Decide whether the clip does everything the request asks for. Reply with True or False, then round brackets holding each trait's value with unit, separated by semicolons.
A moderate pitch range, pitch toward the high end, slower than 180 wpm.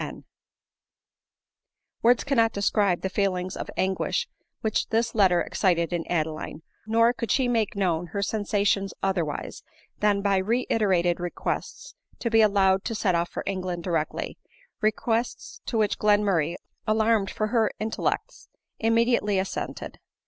True (3.5 semitones; 200 Hz; 140 wpm)